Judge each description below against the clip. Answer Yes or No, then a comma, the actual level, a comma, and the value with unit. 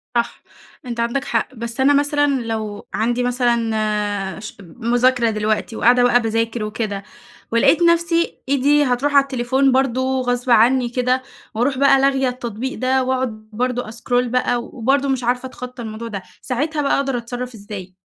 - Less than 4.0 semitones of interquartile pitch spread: Yes, narrow, 2.6 semitones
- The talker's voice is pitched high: Yes, high, 245 Hz